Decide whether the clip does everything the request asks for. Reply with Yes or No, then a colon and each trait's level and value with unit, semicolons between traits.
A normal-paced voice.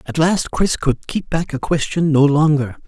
No: fast, 210 wpm